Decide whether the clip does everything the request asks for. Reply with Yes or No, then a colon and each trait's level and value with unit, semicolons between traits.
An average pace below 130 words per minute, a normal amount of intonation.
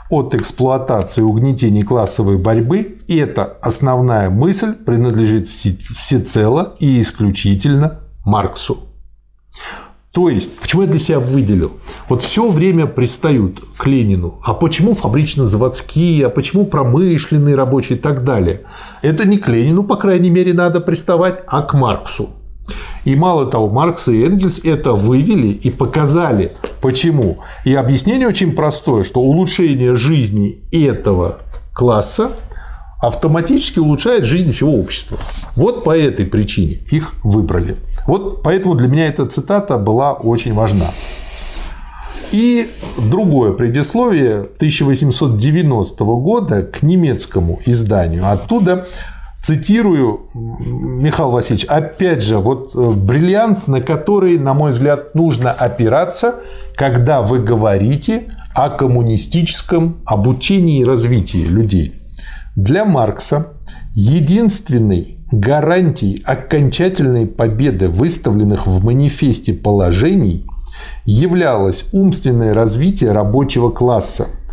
No: slow, 110 wpm; wide, 7.0 semitones